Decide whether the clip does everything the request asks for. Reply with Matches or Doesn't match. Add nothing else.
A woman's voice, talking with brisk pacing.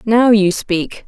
Doesn't match